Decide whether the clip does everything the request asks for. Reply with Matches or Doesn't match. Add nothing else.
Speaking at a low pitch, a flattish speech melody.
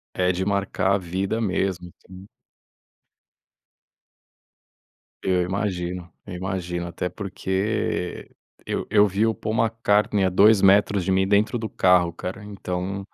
Matches